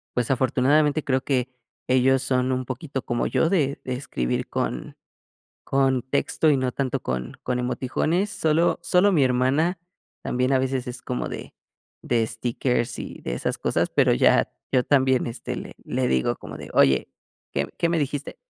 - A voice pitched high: No, low, 130 Hz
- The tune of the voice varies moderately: No, narrow, 2.3 semitones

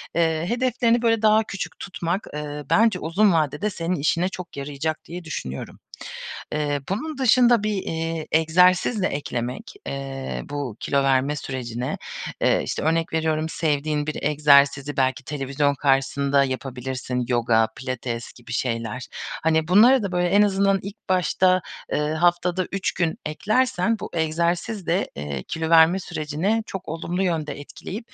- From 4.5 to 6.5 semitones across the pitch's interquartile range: Yes, average, 5.1 semitones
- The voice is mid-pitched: Yes, medium, 160 Hz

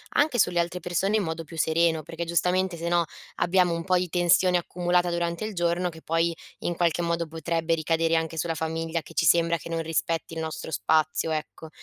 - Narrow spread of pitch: Yes, narrow, 1.3 semitones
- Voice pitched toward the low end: No, medium, 170 Hz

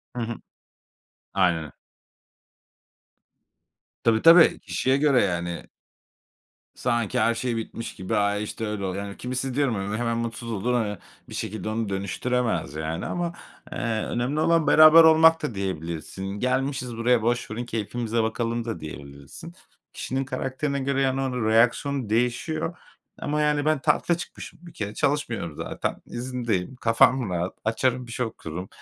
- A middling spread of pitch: Yes, average, 4.6 semitones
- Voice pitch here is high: No, low, 120 Hz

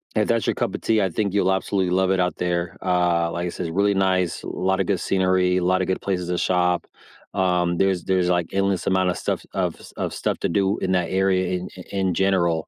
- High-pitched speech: No, very low, 95 Hz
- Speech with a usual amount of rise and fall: No, narrow, 1.3 semitones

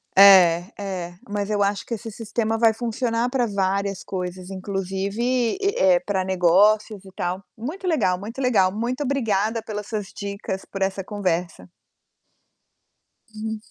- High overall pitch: Yes, high, 200 Hz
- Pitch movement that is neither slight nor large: Yes, average, 3.1 semitones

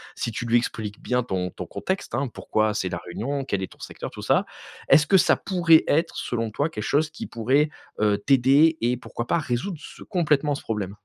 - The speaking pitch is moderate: No, low, 125 Hz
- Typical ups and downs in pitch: No, wide, 6.0 semitones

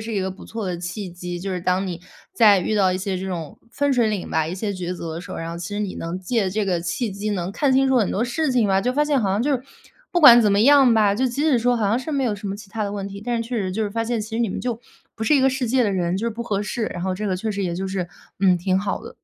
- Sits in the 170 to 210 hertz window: Yes, high, 205 Hz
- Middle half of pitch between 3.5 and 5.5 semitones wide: Yes, average, 4.1 semitones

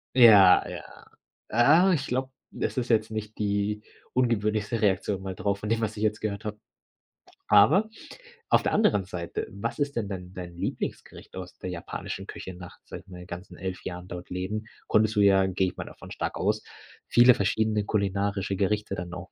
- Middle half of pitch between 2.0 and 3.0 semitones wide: Yes, average, 2.7 semitones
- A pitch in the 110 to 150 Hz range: No, low, 100 Hz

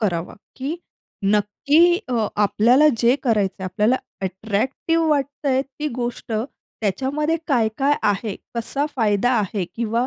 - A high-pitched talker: Yes, high, 235 Hz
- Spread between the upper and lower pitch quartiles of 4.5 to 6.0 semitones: Yes, average, 4.9 semitones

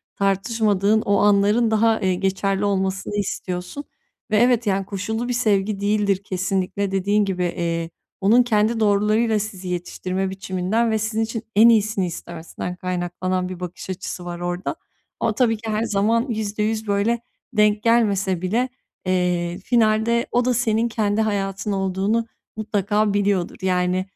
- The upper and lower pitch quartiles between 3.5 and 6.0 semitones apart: No, average, 2.8 semitones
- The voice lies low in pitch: No, high, 205 Hz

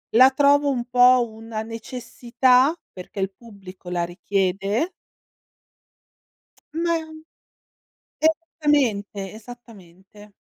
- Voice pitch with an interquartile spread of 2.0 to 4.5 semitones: No, average, 5.0 semitones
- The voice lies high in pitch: Yes, high, 230 Hz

